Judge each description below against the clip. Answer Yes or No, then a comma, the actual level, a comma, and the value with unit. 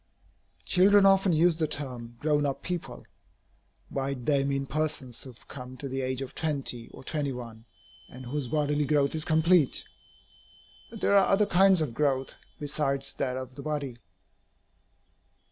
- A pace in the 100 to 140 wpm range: No, average, 160 wpm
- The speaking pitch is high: No, medium, 145 Hz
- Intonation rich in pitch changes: No, average, 3.2 semitones